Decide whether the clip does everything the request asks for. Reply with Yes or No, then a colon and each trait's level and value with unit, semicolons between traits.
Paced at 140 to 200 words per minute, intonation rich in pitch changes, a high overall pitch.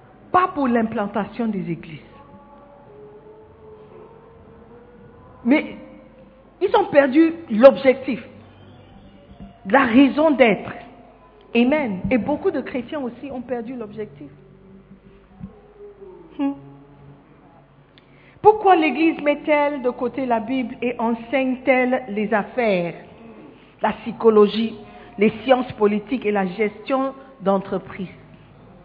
No: slow, 90 wpm; wide, 6.0 semitones; high, 230 Hz